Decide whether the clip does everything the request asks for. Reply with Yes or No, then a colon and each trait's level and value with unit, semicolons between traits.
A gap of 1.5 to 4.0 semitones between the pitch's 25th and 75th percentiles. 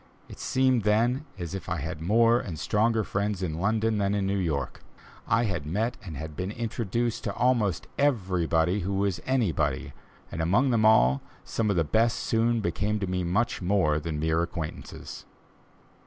No: average, 5.1 semitones